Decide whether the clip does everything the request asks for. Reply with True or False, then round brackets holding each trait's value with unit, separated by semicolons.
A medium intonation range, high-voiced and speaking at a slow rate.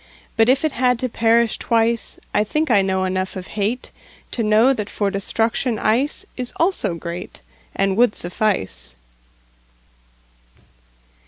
True (4.4 semitones; 220 Hz; 115 wpm)